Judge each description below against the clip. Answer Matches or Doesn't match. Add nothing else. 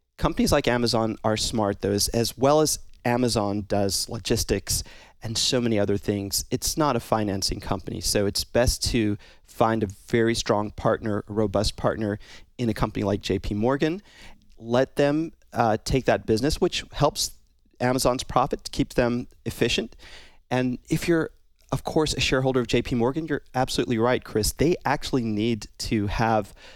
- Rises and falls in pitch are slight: Doesn't match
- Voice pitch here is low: Matches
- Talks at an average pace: Matches